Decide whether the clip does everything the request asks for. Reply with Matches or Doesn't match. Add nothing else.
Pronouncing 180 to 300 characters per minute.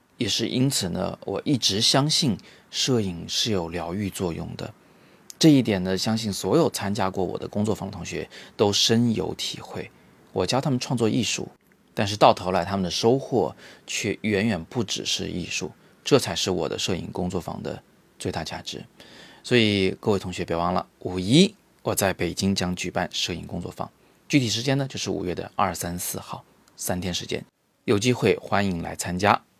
Matches